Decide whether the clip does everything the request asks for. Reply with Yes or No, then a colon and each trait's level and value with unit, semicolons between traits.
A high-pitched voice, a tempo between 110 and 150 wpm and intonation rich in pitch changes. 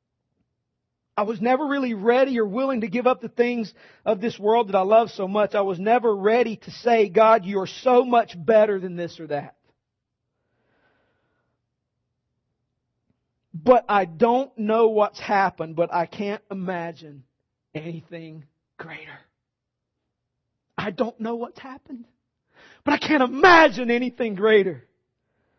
Yes: high, 205 Hz; average, 140 wpm; wide, 8.2 semitones